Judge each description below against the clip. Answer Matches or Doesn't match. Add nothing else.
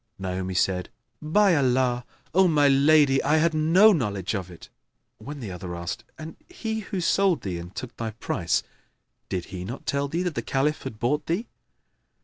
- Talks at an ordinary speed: Matches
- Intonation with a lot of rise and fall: Matches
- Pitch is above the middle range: Doesn't match